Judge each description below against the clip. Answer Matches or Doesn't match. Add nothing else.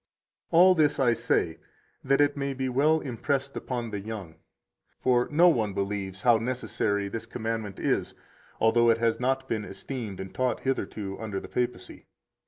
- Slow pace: Doesn't match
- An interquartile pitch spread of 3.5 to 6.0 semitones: Matches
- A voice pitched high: Doesn't match